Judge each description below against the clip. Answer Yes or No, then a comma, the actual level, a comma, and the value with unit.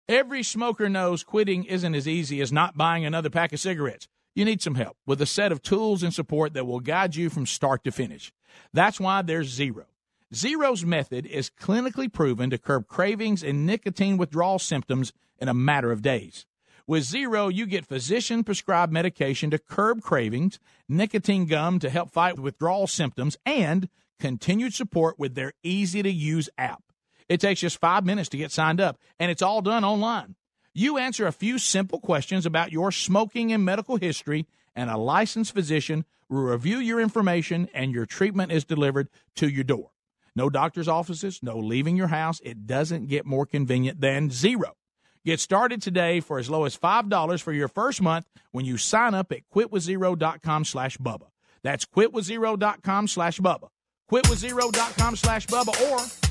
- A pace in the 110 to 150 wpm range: No, average, 180 wpm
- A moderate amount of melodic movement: No, wide, 5.7 semitones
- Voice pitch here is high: No, medium, 175 Hz